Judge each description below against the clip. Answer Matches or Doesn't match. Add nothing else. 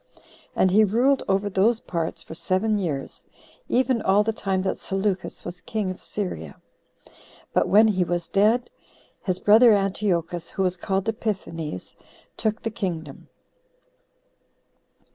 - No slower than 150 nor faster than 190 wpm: Doesn't match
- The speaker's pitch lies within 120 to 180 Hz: Doesn't match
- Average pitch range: Matches